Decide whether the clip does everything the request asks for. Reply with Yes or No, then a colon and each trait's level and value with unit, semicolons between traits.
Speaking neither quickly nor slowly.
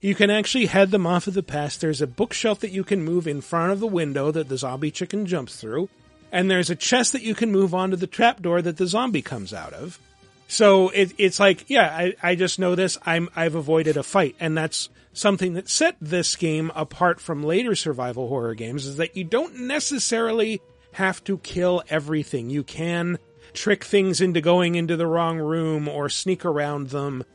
No: fast, 210 wpm